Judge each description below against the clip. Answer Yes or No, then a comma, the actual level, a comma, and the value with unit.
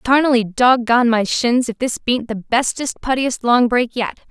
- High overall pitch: Yes, high, 240 Hz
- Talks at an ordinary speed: Yes, average, 180 wpm